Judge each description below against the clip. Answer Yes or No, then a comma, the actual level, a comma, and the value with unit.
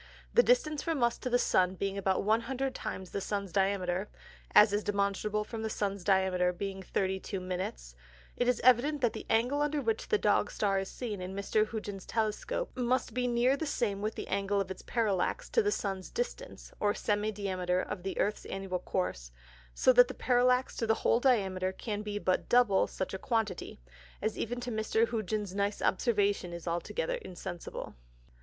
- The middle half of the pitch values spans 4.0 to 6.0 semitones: Yes, average, 4.3 semitones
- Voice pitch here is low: No, high, 205 Hz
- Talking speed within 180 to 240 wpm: Yes, average, 190 wpm